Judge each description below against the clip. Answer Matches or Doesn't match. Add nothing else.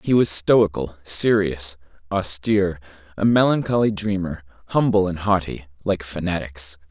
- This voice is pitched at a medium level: Doesn't match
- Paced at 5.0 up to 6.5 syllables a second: Doesn't match